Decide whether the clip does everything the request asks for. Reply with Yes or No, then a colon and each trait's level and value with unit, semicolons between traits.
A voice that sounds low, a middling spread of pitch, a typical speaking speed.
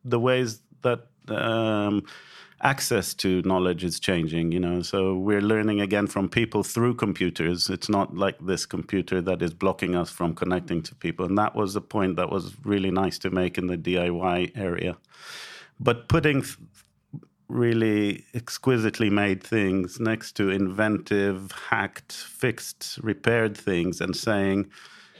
Yes: low, 100 Hz; average, 3.4 semitones; average, 150 wpm